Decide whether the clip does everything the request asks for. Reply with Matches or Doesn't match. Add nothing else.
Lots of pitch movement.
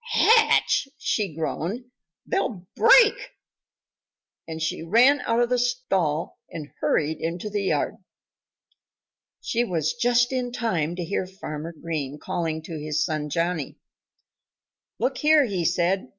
Matches